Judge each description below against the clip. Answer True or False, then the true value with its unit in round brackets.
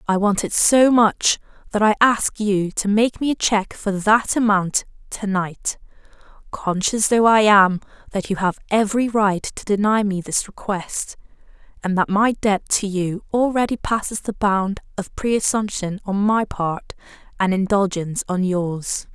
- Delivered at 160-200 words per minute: True (165 wpm)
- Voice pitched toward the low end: False (205 Hz)